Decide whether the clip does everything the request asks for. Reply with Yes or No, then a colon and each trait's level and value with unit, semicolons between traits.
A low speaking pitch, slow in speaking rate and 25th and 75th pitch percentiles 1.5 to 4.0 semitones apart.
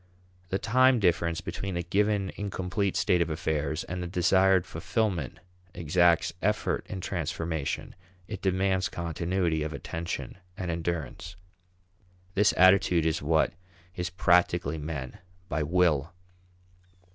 Yes: very low, 85 Hz; slow, 120 wpm; narrow, 2.5 semitones